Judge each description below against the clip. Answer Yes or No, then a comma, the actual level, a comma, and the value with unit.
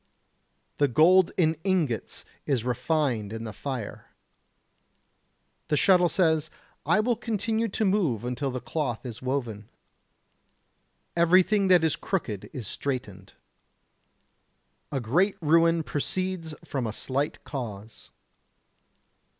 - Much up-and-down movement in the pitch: Yes, wide, 6.9 semitones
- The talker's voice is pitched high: No, medium, 150 Hz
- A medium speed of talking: No, slow, 110 wpm